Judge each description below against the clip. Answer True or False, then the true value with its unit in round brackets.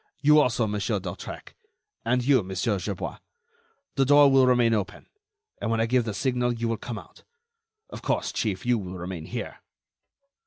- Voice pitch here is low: True (115 Hz)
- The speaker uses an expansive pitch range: False (3.9 semitones)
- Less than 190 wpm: True (170 wpm)